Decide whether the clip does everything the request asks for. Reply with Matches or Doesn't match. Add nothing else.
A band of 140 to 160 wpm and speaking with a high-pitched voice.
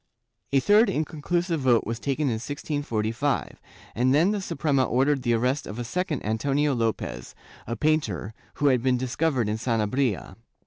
Doesn't match